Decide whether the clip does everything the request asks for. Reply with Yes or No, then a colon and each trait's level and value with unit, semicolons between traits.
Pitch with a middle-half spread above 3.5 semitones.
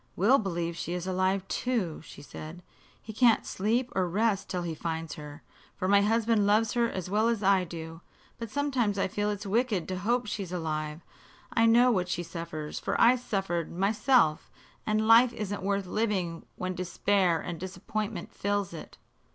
Yes: average, 4.3 semitones